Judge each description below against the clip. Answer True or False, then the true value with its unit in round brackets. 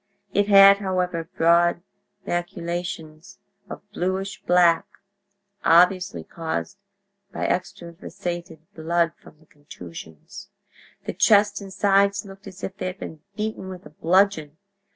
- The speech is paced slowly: True (115 wpm)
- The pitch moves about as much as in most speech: True (3.1 semitones)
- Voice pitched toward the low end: False (175 Hz)